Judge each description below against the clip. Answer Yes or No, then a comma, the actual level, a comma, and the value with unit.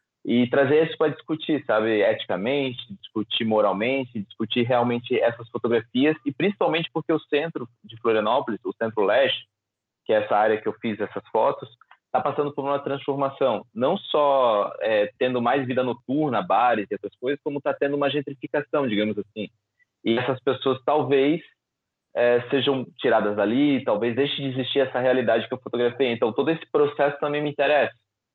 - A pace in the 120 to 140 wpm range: No, average, 165 wpm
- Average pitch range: Yes, average, 4.0 semitones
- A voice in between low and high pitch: No, low, 130 Hz